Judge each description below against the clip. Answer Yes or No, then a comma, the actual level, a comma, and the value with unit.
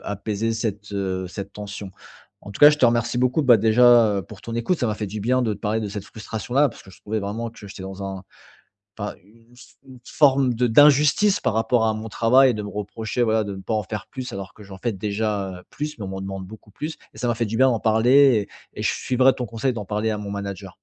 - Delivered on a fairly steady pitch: No, average, 3.3 semitones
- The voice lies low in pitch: Yes, low, 110 Hz